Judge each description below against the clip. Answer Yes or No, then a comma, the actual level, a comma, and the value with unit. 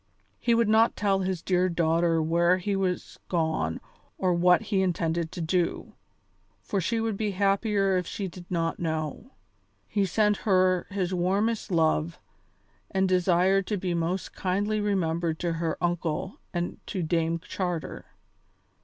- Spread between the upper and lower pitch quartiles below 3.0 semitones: Yes, narrow, 2.6 semitones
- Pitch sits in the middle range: Yes, medium, 180 Hz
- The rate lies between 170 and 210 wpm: No, average, 150 wpm